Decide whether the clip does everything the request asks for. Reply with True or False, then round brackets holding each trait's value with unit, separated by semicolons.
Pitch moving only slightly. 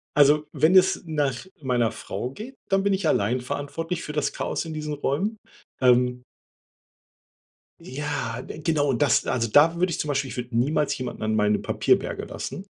False (4.4 semitones)